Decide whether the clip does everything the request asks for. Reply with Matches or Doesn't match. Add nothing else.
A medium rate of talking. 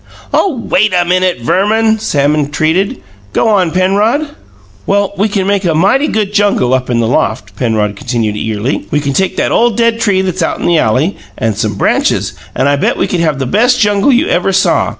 Doesn't match